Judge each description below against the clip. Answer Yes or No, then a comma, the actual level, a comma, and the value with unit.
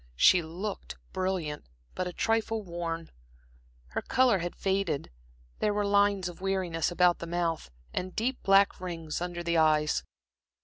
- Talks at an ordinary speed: Yes, average, 145 wpm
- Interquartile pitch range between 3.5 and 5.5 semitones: No, average, 3.0 semitones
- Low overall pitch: No, medium, 180 Hz